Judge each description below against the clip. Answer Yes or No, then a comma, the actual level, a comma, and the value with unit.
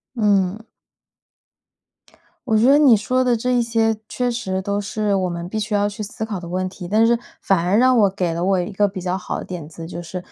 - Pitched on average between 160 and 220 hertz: Yes, high, 205 Hz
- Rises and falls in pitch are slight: No, average, 3.5 semitones